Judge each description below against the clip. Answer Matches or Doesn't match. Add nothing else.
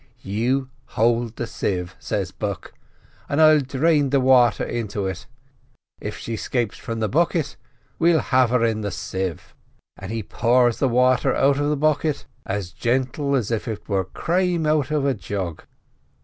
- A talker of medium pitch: Doesn't match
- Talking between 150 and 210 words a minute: Matches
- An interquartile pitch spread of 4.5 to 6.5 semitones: Matches